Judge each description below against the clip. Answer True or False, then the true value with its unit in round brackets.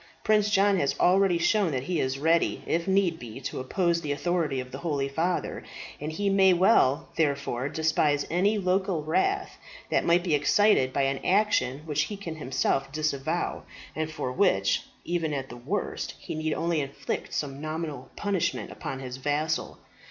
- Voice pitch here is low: False (155 Hz)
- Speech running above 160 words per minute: True (175 wpm)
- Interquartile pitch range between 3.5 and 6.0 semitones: True (4.8 semitones)